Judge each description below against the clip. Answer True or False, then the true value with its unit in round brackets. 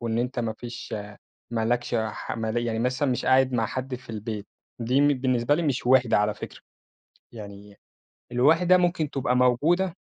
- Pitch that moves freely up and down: False (3.0 semitones)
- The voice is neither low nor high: False (125 Hz)